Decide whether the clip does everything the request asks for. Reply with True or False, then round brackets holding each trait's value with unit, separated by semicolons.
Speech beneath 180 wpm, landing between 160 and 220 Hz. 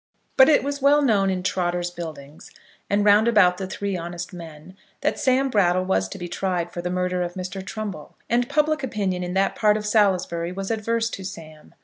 False (205 wpm; 190 Hz)